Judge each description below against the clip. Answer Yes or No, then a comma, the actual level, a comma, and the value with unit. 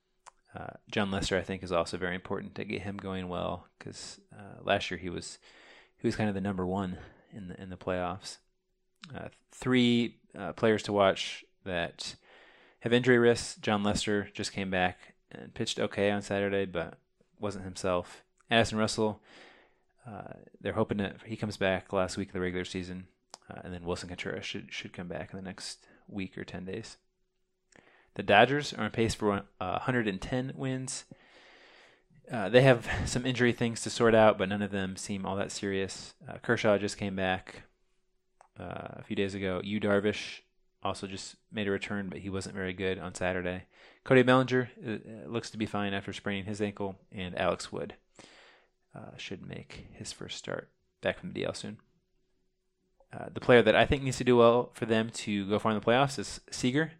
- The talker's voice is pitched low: Yes, low, 105 Hz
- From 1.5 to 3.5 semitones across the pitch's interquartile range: No, average, 3.9 semitones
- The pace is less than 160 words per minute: No, average, 190 wpm